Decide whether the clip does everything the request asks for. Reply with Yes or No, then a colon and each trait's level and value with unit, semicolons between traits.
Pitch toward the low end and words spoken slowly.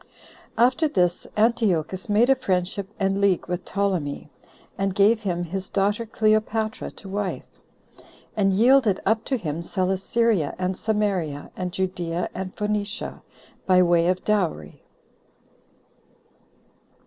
No: high, 195 Hz; slow, 125 wpm